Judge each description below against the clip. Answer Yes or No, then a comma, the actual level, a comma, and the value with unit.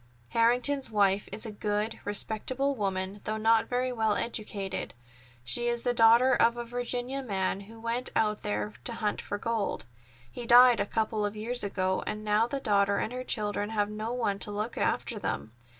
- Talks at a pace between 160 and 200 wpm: Yes, average, 185 wpm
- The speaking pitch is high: Yes, high, 220 Hz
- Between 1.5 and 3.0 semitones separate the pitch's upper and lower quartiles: Yes, average, 2.7 semitones